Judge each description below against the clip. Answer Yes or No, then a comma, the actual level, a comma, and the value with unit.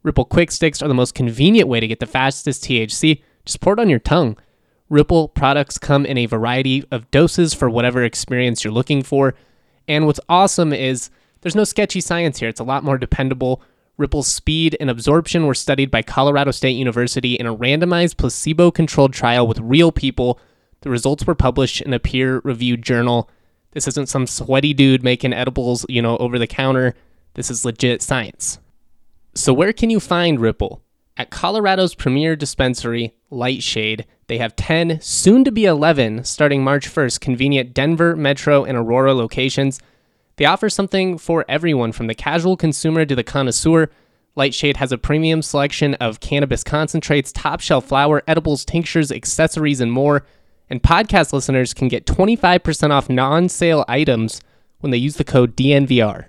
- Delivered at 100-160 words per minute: No, average, 170 wpm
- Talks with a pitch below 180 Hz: Yes, low, 135 Hz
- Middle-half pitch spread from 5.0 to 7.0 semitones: No, average, 4.2 semitones